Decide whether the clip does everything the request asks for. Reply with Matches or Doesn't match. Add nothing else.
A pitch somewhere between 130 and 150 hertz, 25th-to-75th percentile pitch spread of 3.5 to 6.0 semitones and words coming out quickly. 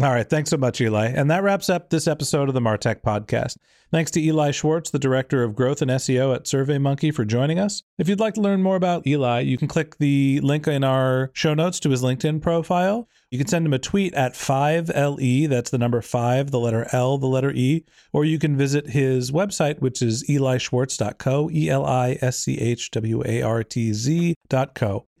Matches